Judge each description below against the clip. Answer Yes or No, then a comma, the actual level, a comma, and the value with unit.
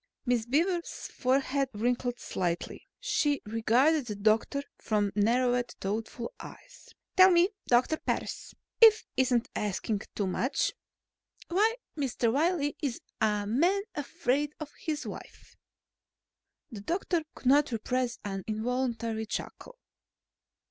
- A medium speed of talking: No, slow, 120 wpm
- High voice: Yes, very high, 250 Hz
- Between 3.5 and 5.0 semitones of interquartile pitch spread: No, wide, 5.4 semitones